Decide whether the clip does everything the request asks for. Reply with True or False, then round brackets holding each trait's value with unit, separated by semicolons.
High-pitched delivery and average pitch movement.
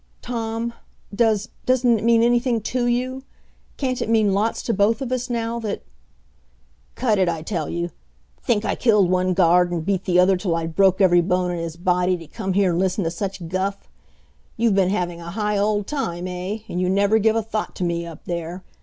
True (195 Hz; 4.3 semitones)